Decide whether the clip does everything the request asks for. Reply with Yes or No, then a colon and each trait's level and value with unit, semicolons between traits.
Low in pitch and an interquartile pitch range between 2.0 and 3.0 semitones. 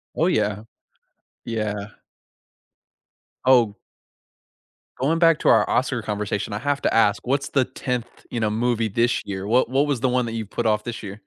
No: low, 115 Hz; average, 3.5 semitones